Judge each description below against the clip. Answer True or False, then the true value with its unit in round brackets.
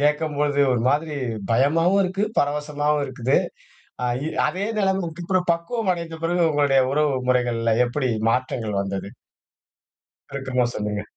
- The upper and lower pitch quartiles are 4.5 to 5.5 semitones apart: True (4.9 semitones)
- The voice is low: False (145 Hz)